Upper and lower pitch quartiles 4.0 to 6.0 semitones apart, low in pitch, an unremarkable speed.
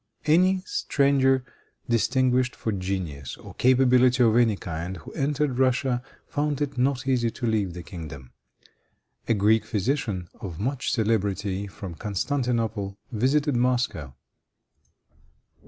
No: average, 5.1 semitones; low, 120 Hz; slow, 120 wpm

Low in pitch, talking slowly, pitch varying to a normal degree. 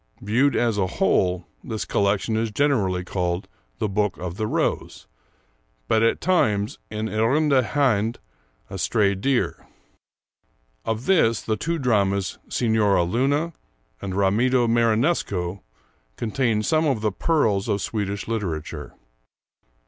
Yes: low, 110 Hz; slow, 125 wpm; average, 3.8 semitones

